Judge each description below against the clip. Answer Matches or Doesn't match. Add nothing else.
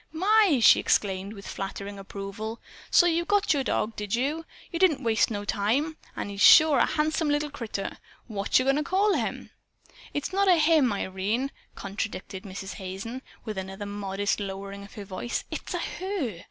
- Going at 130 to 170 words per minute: Doesn't match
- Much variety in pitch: Matches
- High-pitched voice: Matches